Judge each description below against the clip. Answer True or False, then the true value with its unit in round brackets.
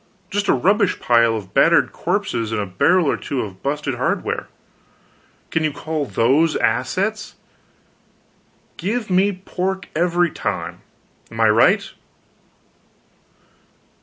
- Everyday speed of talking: False (120 wpm)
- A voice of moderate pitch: True (155 Hz)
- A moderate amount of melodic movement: False (8.1 semitones)